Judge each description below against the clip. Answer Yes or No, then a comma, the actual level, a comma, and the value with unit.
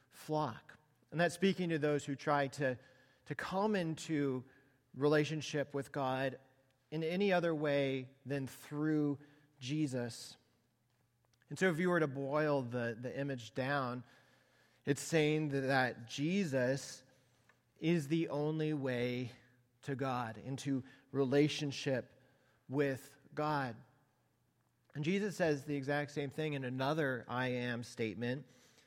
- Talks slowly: Yes, slow, 125 wpm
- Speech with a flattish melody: No, average, 3.0 semitones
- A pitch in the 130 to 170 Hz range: Yes, low, 135 Hz